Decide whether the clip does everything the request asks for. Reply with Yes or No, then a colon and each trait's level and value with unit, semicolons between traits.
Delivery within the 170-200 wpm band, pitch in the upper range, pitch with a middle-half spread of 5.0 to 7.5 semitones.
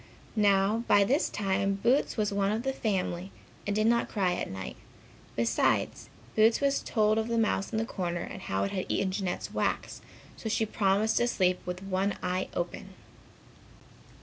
No: average, 175 wpm; high, 200 Hz; average, 3.0 semitones